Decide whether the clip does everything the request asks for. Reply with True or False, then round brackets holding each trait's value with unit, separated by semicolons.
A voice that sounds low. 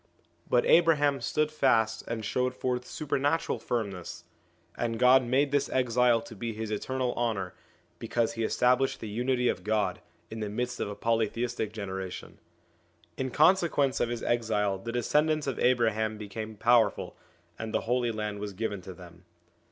True (115 Hz)